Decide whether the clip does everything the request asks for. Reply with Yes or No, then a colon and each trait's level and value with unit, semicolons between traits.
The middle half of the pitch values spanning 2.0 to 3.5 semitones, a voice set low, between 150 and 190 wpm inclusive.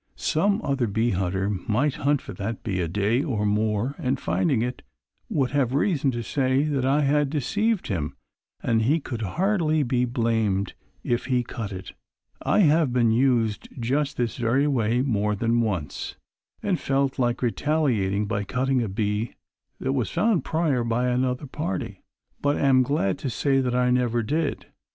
No: average, 4.2 semitones; low, 125 Hz; average, 170 wpm